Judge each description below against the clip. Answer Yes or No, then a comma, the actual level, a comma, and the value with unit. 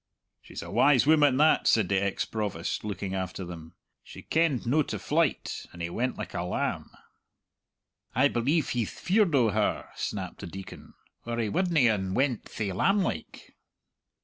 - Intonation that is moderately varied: No, wide, 7.3 semitones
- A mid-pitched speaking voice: No, low, 120 Hz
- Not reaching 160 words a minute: No, average, 170 wpm